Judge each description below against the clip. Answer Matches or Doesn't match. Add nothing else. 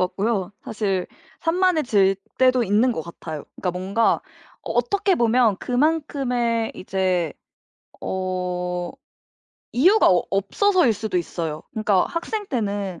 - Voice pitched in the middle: Doesn't match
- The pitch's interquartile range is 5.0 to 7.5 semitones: Matches